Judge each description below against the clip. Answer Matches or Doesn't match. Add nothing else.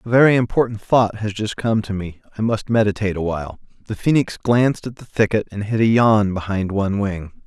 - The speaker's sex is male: Matches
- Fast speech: Matches